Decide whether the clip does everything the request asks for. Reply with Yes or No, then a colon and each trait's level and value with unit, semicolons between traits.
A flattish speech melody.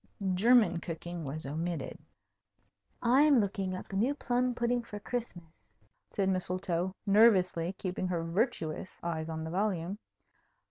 No: average, 5.1 semitones